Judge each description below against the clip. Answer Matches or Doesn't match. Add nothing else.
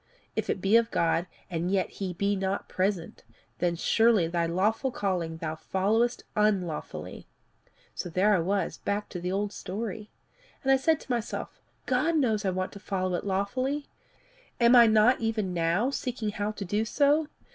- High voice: Matches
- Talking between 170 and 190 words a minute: Matches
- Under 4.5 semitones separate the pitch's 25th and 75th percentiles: Matches